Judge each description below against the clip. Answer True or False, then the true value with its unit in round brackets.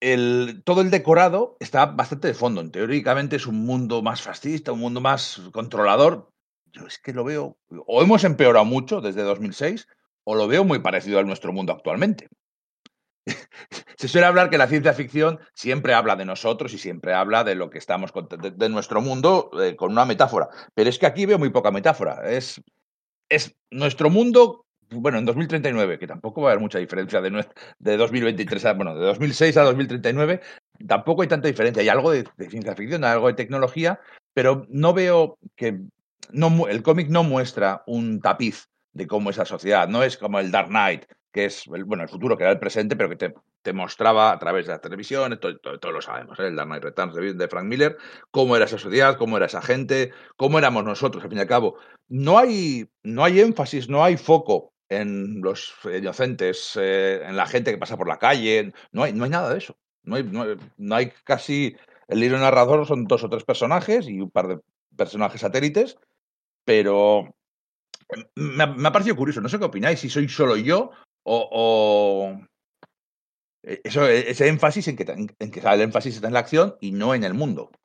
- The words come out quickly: True (205 wpm)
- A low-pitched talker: True (130 Hz)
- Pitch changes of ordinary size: False (6.7 semitones)